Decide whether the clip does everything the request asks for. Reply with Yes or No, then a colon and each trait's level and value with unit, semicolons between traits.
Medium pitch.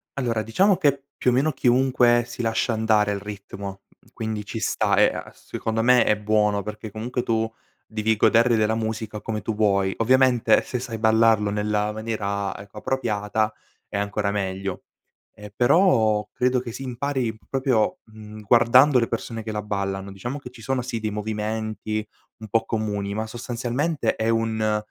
No: low, 110 Hz